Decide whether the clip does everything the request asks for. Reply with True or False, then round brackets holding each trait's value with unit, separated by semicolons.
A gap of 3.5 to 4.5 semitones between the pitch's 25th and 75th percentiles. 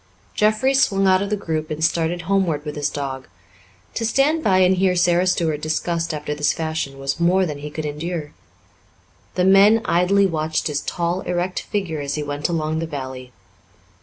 True (4.0 semitones)